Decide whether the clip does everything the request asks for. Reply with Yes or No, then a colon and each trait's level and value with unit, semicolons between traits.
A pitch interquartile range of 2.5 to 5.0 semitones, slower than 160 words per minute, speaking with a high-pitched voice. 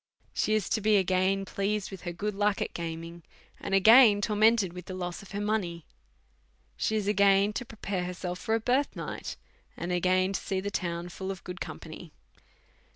No: average, 2.8 semitones; average, 200 wpm; high, 195 Hz